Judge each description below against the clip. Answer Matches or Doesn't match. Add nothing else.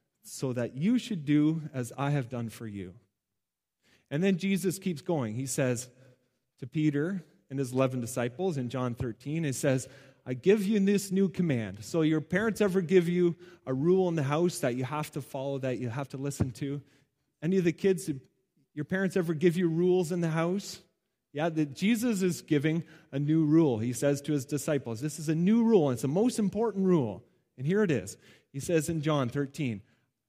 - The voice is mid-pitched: Matches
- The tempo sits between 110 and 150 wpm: Doesn't match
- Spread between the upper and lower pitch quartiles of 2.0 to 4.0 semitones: Doesn't match